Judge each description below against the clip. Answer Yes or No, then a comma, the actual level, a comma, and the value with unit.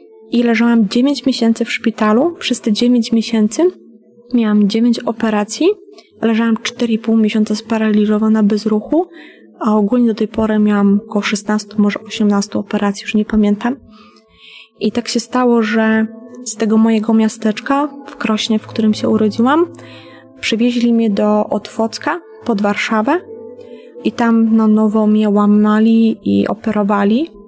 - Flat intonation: Yes, narrow, 2.1 semitones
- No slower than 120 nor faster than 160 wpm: Yes, average, 135 wpm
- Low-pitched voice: No, high, 220 Hz